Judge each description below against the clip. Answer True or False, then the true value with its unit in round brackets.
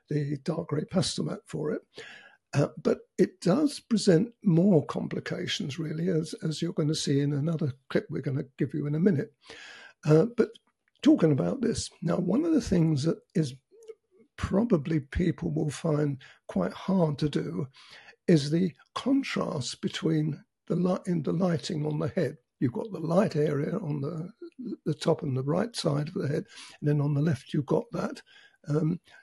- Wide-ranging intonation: False (5.0 semitones)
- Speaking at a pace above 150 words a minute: True (185 wpm)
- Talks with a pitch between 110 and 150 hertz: False (165 Hz)